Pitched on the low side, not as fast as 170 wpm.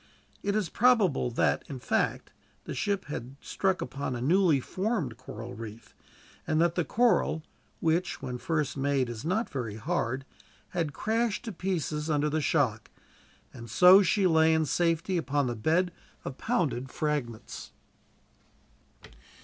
No: medium, 155 Hz; average, 145 wpm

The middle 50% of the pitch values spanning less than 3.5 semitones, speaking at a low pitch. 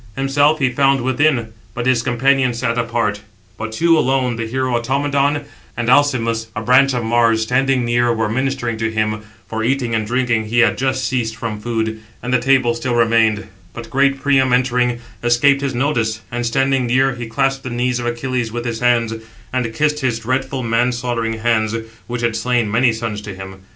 Yes: narrow, 2.5 semitones; low, 120 Hz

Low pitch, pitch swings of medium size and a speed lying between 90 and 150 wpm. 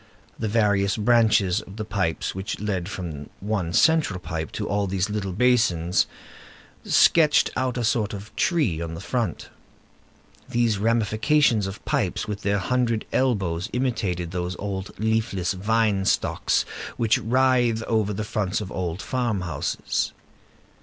Yes: low, 105 Hz; average, 3.7 semitones; average, 140 wpm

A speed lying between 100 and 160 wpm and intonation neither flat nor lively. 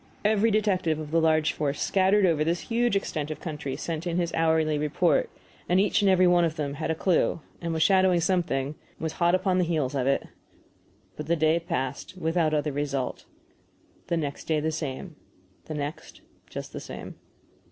No: average, 190 wpm; average, 3.2 semitones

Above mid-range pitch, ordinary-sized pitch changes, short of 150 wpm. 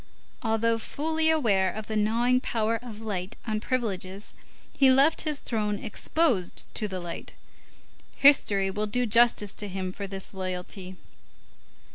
Yes: high, 215 Hz; average, 4.0 semitones; average, 140 wpm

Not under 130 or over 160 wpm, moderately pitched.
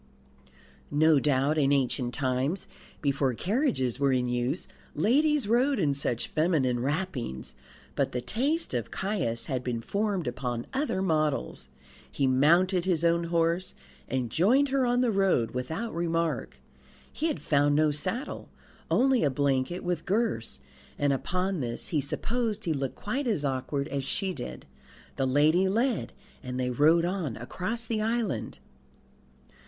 Yes: average, 150 wpm; medium, 155 Hz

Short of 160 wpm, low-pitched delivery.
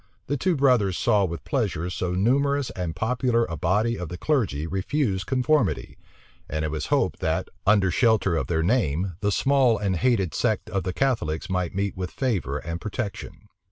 No: average, 180 wpm; low, 100 Hz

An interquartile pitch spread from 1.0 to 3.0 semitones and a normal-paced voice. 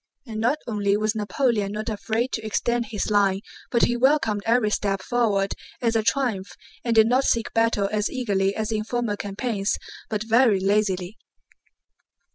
Yes: narrow, 2.6 semitones; average, 165 wpm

